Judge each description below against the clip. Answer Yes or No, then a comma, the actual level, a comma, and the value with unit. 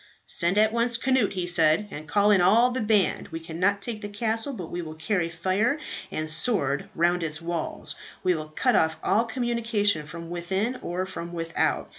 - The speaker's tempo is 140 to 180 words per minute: No, average, 190 wpm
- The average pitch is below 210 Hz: Yes, medium, 185 Hz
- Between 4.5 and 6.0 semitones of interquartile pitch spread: Yes, average, 4.8 semitones